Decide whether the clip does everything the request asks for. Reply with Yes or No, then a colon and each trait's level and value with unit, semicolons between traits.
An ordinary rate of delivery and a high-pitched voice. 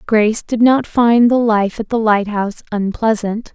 Yes: average, 170 wpm; high, 220 Hz